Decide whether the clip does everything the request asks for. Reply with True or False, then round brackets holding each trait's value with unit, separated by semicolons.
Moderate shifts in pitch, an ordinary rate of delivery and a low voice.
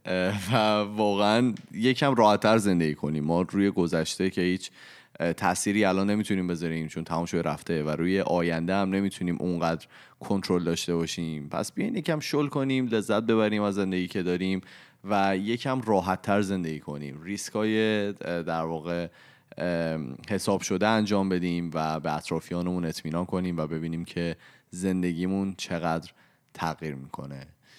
True (3.6 semitones; 140 wpm; 90 Hz)